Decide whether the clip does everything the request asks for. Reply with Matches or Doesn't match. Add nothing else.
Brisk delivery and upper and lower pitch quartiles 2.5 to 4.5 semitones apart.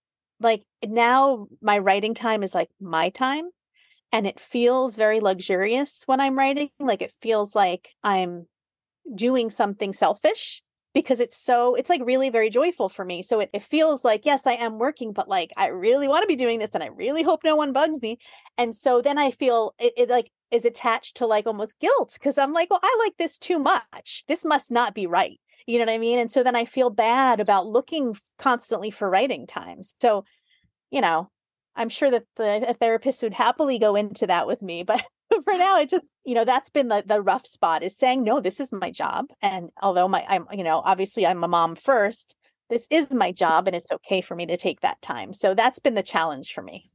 Doesn't match